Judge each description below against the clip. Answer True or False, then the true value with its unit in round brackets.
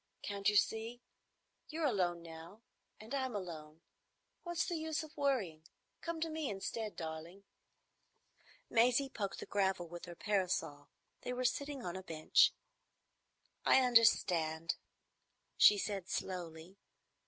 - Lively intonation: True (6.6 semitones)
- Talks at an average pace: False (130 wpm)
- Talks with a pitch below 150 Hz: False (200 Hz)